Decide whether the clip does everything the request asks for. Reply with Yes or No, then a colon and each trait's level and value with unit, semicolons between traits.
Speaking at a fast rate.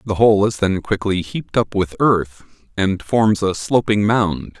No: average, 185 wpm